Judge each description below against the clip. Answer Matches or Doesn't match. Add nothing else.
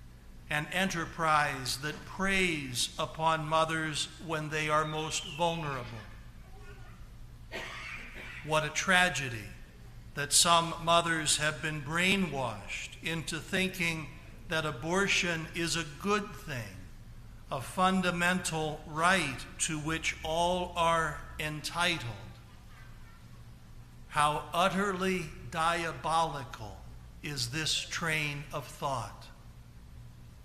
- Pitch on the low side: Doesn't match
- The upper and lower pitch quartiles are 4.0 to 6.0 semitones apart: Matches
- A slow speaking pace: Matches